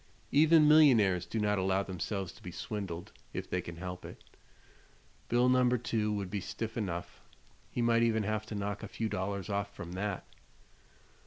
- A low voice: Yes, low, 105 Hz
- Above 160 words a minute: Yes, average, 175 wpm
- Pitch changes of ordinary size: Yes, average, 3.6 semitones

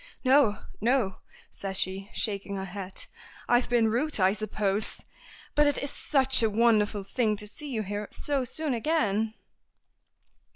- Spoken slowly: No, average, 150 wpm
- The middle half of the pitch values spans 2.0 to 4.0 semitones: No, average, 4.5 semitones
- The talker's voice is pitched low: No, high, 220 Hz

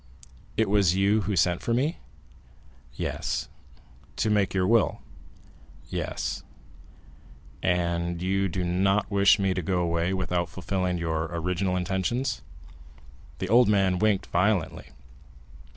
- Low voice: Yes, very low, 95 Hz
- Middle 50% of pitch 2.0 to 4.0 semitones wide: Yes, narrow, 2.4 semitones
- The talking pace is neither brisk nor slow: No, slow, 120 wpm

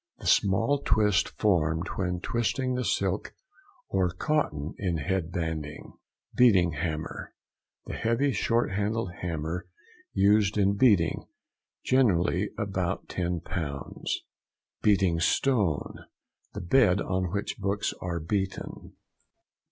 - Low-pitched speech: Yes, very low, 95 Hz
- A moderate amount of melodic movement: Yes, average, 3.8 semitones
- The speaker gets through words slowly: Yes, slow, 105 wpm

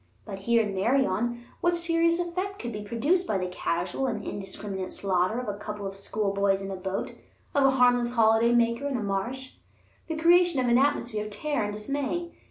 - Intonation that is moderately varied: No, wide, 5.7 semitones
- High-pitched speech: Yes, high, 235 Hz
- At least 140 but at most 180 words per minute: No, average, 195 wpm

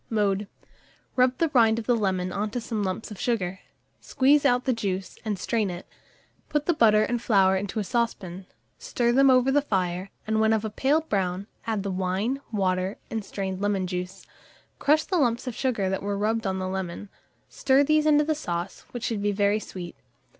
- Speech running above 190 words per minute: Yes, average, 200 wpm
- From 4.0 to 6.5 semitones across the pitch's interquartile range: Yes, average, 4.4 semitones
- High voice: Yes, high, 210 Hz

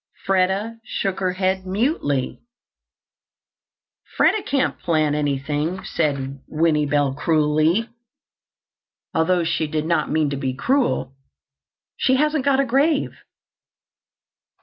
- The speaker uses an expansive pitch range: Yes, wide, 7.3 semitones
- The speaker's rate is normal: No, slow, 105 wpm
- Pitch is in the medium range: Yes, medium, 165 Hz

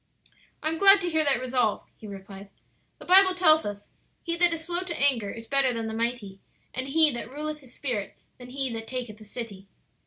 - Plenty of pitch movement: Yes, wide, 6.0 semitones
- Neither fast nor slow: No, fast, 215 wpm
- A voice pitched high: Yes, very high, 255 Hz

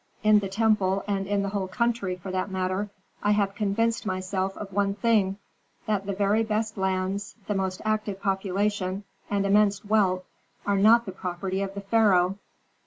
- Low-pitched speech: No, high, 200 Hz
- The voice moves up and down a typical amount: No, narrow, 1.7 semitones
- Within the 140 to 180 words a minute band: Yes, average, 175 wpm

